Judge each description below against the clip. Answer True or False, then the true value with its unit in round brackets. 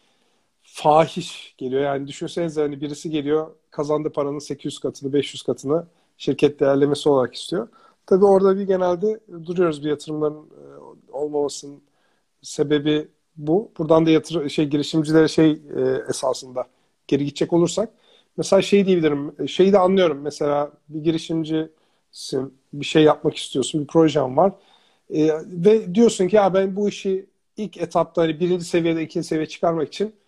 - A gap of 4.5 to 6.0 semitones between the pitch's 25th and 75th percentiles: False (3.3 semitones)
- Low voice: False (160 Hz)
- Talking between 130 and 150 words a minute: True (140 wpm)